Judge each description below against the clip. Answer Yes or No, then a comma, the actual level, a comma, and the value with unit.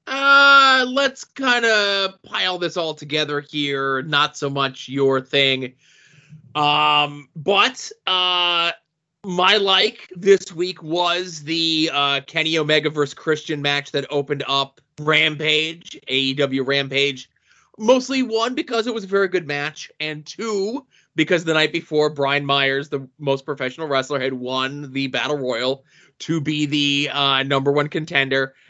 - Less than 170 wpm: Yes, average, 140 wpm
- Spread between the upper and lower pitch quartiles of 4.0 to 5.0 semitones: Yes, average, 4.4 semitones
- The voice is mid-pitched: Yes, medium, 150 Hz